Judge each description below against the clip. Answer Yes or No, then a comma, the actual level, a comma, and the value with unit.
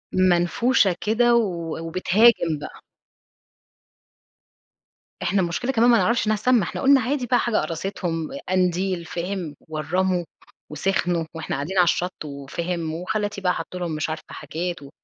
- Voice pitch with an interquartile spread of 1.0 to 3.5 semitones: No, average, 4.3 semitones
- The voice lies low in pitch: No, medium, 180 Hz